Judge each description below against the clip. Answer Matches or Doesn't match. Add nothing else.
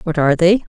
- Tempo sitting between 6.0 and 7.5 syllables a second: Matches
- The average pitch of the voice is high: Doesn't match